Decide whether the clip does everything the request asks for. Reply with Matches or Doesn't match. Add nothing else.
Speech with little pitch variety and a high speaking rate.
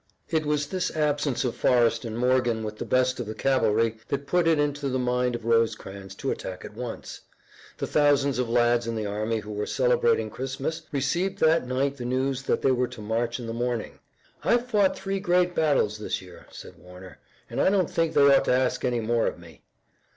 Doesn't match